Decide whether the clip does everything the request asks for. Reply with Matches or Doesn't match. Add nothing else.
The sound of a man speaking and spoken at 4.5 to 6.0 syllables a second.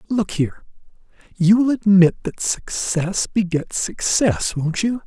Doesn't match